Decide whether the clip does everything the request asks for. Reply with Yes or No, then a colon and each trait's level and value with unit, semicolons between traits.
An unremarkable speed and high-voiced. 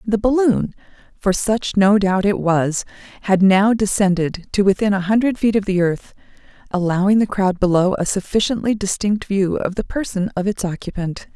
Yes: average, 175 wpm; high, 200 Hz